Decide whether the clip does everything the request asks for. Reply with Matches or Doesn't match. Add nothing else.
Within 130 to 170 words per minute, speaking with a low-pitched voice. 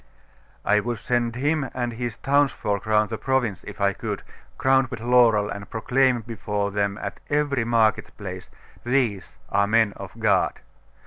Matches